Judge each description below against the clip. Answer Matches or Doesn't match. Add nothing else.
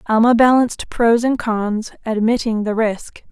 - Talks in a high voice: Matches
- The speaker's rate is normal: Matches